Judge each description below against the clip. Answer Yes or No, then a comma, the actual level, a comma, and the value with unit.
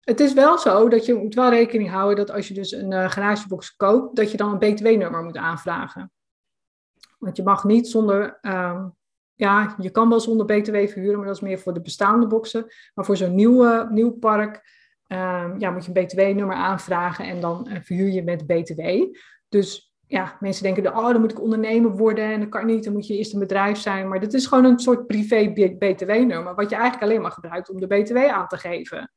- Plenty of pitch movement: No, average, 2.9 semitones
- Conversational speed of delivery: No, fast, 220 wpm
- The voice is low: No, high, 205 Hz